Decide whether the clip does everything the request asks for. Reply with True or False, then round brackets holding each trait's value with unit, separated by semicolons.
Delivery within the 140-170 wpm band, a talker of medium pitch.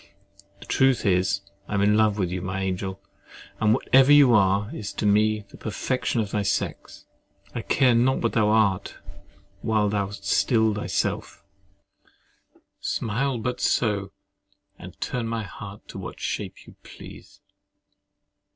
False (150 wpm; 105 Hz)